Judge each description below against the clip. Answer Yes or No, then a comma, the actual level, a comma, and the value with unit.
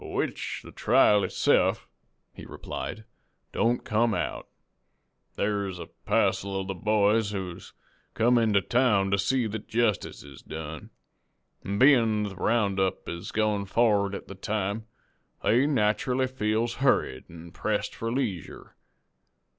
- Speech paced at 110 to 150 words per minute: Yes, slow, 135 wpm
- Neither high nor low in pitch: No, low, 105 Hz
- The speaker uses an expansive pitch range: No, average, 2.9 semitones